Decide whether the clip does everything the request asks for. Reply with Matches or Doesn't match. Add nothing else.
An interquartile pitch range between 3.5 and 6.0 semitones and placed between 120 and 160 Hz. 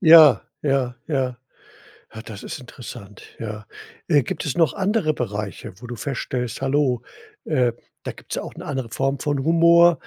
Matches